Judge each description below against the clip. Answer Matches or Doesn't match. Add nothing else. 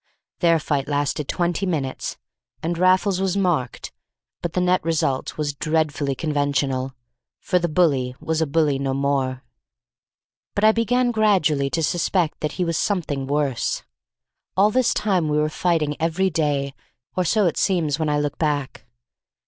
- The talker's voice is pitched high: Doesn't match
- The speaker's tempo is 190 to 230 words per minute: Doesn't match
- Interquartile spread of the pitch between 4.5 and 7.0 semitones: Doesn't match